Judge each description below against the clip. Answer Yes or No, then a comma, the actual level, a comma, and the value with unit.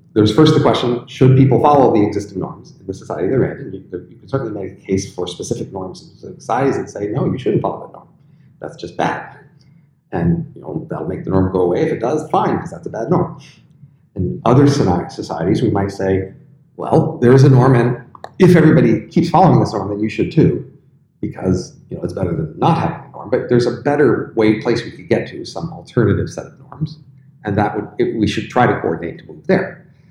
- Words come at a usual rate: No, fast, 225 wpm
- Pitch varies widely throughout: Yes, wide, 5.7 semitones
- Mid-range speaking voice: No, low, 130 Hz